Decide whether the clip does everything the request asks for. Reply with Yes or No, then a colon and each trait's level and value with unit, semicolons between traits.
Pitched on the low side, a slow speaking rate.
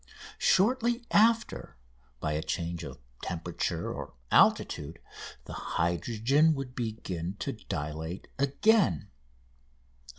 Yes: low, 110 Hz; slow, 95 wpm